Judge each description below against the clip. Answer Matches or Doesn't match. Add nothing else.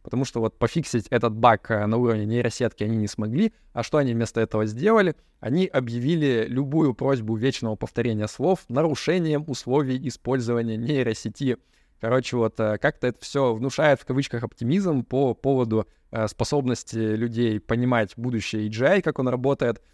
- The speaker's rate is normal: Matches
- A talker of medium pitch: Doesn't match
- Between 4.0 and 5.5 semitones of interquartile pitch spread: Doesn't match